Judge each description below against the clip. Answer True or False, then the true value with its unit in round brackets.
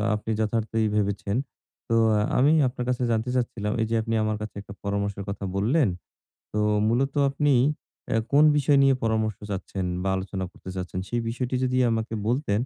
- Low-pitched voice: True (110 Hz)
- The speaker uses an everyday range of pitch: True (3.7 semitones)